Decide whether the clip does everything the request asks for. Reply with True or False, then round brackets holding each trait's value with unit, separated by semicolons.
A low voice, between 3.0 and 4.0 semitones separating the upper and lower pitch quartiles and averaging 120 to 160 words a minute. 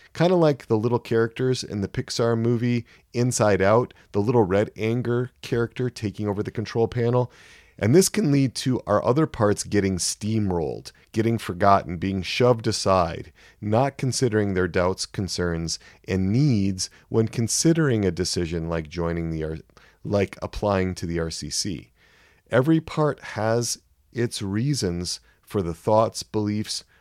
False (110 Hz; 4.4 semitones; 145 wpm)